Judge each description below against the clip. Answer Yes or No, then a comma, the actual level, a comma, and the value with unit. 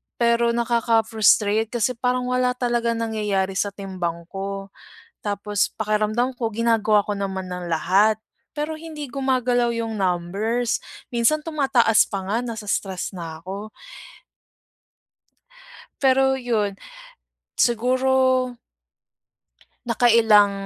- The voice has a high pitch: Yes, high, 225 Hz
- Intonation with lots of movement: No, average, 3.6 semitones